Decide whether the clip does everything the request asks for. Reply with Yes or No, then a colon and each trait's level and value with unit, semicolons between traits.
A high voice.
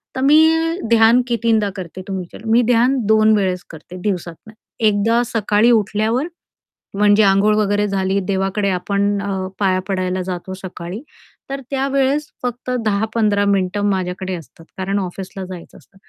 Yes: high, 205 Hz